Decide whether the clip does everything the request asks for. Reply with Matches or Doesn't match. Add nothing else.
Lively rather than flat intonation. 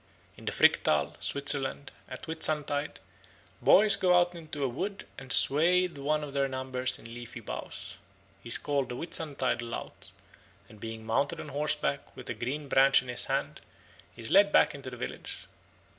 Doesn't match